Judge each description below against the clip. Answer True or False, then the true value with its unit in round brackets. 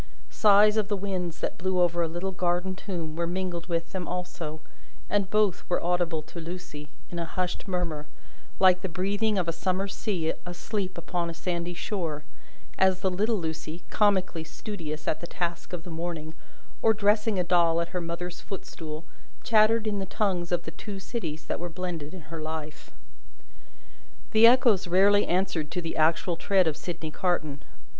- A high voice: False (180 Hz)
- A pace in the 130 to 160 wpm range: False (180 wpm)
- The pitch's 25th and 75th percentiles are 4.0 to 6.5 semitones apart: False (2.5 semitones)